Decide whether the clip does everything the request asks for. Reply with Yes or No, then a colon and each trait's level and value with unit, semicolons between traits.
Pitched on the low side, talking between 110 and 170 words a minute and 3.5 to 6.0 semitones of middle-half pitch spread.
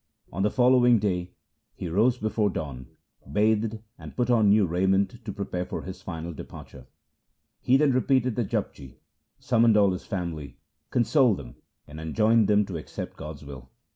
Yes: low, 100 Hz; average, 165 wpm; average, 5.3 semitones